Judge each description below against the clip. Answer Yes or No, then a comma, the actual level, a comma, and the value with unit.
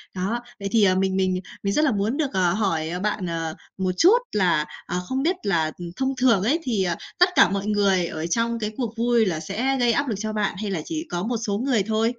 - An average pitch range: Yes, average, 4.5 semitones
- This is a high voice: Yes, high, 210 Hz